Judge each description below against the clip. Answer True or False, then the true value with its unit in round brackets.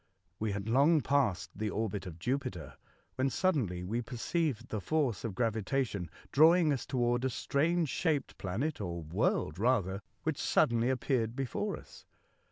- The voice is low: True (120 Hz)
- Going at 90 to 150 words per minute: False (160 wpm)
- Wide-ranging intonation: True (5.7 semitones)